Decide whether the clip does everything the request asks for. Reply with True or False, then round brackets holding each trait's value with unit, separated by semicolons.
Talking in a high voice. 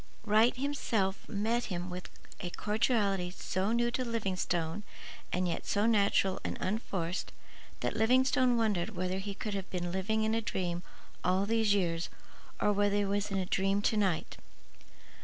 True (200 Hz)